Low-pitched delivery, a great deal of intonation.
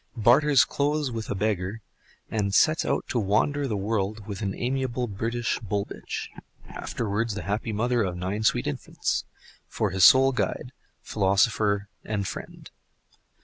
No: low, 110 Hz; average, 3.4 semitones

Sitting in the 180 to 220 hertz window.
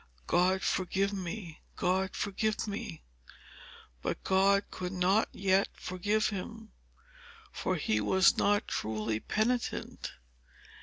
Yes: high, 190 Hz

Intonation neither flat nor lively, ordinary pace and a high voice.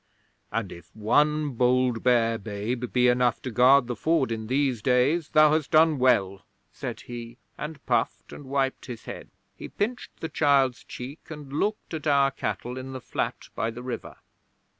No: average, 3.5 semitones; average, 175 wpm; low, 130 Hz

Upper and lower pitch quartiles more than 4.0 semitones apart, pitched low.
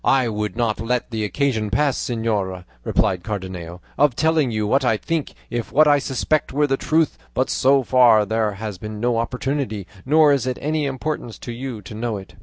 Yes: average, 4.5 semitones; low, 120 Hz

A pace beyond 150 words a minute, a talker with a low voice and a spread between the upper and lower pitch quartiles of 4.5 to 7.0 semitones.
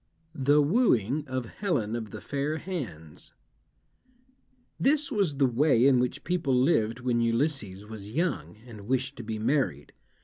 No: average, 145 wpm; low, 130 Hz; average, 5.0 semitones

